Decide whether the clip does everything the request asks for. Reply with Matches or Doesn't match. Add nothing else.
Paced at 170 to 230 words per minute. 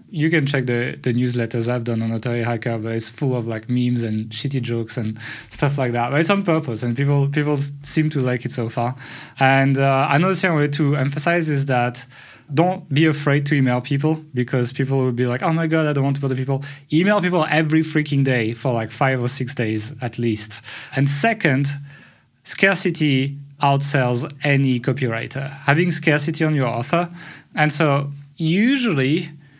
Matches